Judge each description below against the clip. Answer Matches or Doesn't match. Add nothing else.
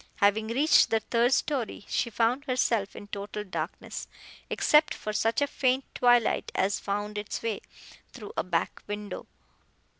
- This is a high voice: Matches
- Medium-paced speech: Matches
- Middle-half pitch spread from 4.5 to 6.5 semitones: Doesn't match